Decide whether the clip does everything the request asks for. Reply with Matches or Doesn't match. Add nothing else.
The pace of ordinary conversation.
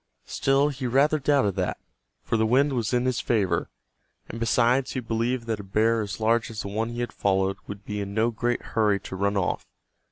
Doesn't match